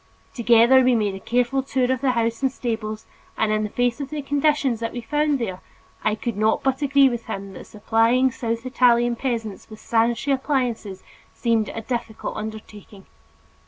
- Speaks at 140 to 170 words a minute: No, average, 180 wpm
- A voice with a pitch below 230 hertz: No, high, 235 Hz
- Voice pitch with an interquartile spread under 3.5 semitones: Yes, average, 3.0 semitones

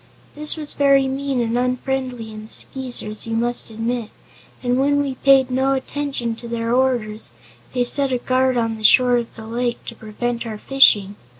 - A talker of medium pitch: No, high, 245 Hz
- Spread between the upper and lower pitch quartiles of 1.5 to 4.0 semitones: Yes, average, 2.7 semitones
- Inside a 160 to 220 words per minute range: Yes, average, 185 wpm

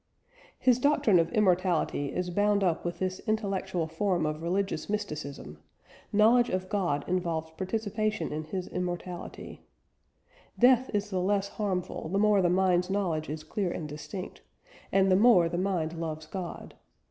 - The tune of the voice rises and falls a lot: No, average, 3.5 semitones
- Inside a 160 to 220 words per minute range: No, average, 150 wpm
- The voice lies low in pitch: No, medium, 185 Hz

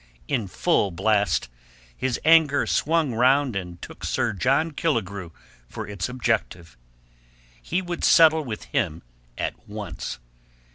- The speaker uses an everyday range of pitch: No, wide, 7.9 semitones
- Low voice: Yes, low, 125 Hz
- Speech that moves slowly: Yes, slow, 125 wpm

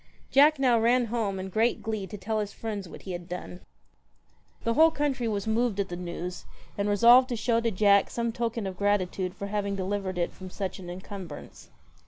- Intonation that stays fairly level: No, average, 3.5 semitones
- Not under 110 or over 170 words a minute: No, fast, 205 wpm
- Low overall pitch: No, high, 205 Hz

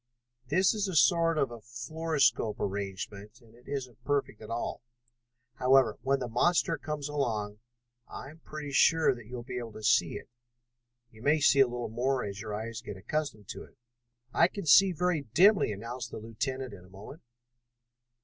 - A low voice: Yes, low, 125 Hz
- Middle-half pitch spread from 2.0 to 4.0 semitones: No, wide, 5.5 semitones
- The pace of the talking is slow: No, average, 185 wpm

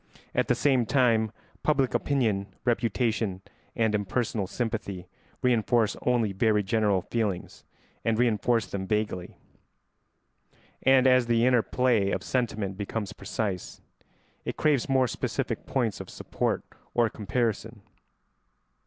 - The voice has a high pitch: No, low, 115 Hz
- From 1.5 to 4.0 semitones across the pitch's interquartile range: Yes, average, 3.2 semitones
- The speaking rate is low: Yes, slow, 120 wpm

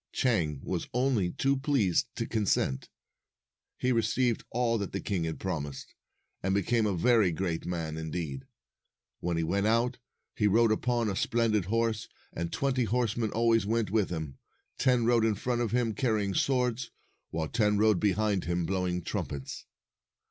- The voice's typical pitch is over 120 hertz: No, low, 105 Hz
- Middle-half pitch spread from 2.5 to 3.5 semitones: No, average, 4.9 semitones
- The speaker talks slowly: No, average, 165 wpm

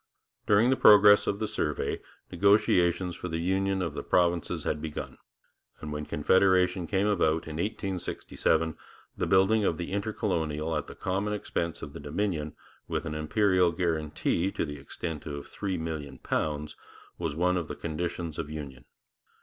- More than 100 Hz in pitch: No, very low, 85 Hz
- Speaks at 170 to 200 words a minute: No, average, 155 wpm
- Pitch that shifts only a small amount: No, average, 3.8 semitones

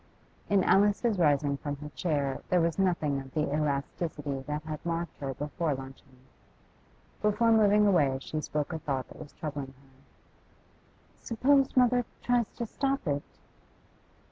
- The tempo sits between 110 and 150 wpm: Yes, average, 145 wpm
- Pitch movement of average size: No, wide, 6.3 semitones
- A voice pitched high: No, medium, 155 Hz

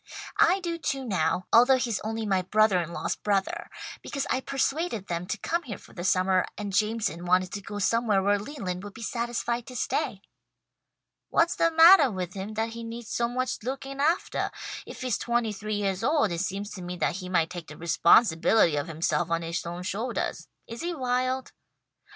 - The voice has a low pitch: No, high, 215 Hz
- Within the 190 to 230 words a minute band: Yes, average, 195 wpm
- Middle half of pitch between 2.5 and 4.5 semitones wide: No, wide, 5.4 semitones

